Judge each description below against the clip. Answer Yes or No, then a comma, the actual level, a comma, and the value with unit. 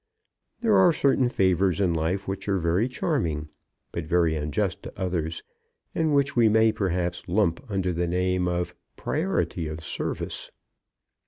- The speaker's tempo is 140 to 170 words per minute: Yes, average, 150 wpm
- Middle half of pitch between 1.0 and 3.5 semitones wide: No, average, 4.6 semitones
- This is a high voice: No, very low, 90 Hz